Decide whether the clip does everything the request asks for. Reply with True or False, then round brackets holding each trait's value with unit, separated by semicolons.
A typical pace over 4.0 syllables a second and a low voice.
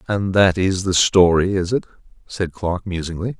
True (5.0 syllables/s; 95 Hz)